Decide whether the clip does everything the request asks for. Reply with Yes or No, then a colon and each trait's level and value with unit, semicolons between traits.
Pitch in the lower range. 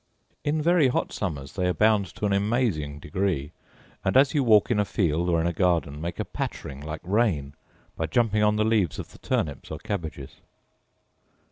Yes: very low, 95 Hz